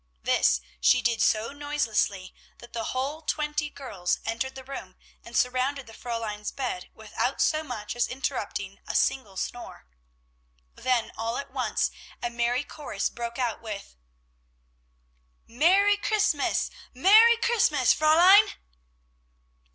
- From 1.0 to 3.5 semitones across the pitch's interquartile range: No, average, 4.8 semitones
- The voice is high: Yes, very high, 255 Hz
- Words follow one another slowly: Yes, slow, 125 wpm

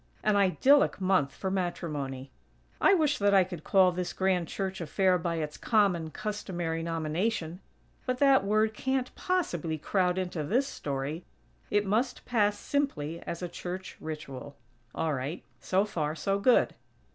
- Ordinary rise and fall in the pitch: Yes, average, 4.5 semitones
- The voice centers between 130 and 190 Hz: Yes, medium, 185 Hz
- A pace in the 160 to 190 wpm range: No, average, 150 wpm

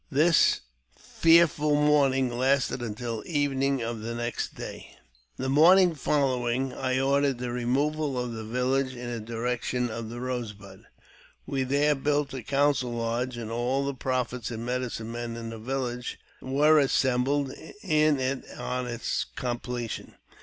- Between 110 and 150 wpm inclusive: Yes, average, 145 wpm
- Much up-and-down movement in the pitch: No, average, 2.7 semitones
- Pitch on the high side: No, low, 130 Hz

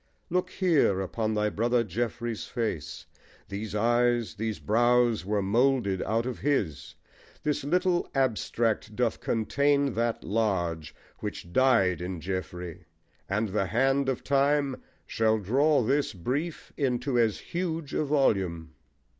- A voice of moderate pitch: No, low, 115 Hz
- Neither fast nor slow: No, slow, 130 wpm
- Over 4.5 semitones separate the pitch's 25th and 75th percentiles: Yes, average, 5.2 semitones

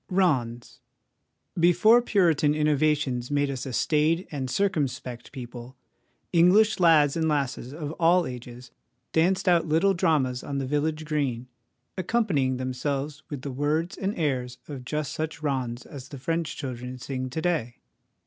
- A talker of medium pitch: Yes, medium, 145 Hz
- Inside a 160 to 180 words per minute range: No, average, 145 wpm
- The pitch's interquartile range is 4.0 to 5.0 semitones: Yes, average, 4.3 semitones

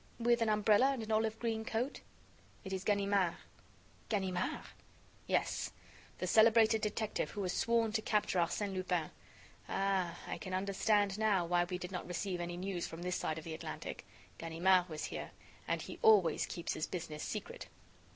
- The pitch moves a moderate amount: Yes, average, 3.6 semitones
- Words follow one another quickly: No, average, 170 wpm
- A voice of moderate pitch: No, high, 195 Hz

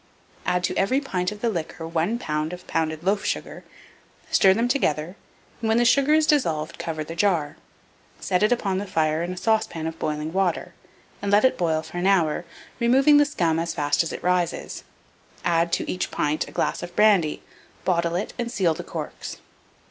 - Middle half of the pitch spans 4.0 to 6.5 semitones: Yes, average, 4.6 semitones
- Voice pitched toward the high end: No, medium, 180 Hz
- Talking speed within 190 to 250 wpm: Yes, average, 195 wpm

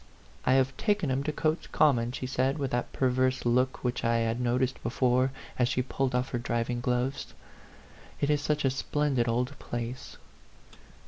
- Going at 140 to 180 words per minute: Yes, average, 175 wpm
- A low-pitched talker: Yes, low, 130 Hz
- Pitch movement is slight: Yes, narrow, 1.8 semitones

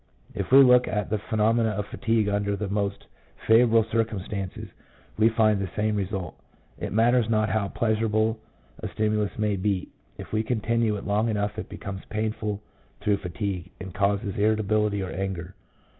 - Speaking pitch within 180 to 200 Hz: No, low, 105 Hz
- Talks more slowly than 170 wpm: Yes, average, 160 wpm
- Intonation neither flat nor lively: No, narrow, 1.7 semitones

